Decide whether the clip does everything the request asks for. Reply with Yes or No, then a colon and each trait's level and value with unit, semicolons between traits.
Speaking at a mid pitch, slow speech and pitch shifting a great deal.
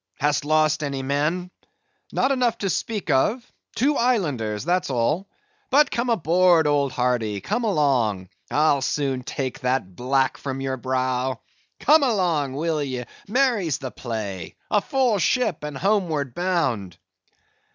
Yes: medium, 150 Hz; slow, 130 wpm; wide, 7.2 semitones